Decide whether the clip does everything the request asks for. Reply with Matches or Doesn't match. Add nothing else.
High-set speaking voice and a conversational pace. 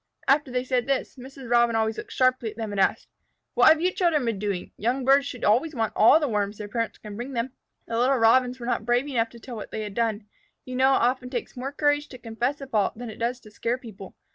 Doesn't match